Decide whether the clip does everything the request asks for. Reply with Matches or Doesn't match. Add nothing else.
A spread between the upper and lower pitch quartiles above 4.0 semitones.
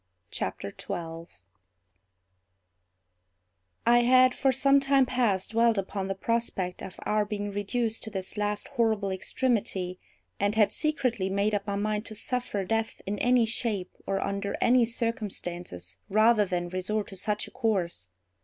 Doesn't match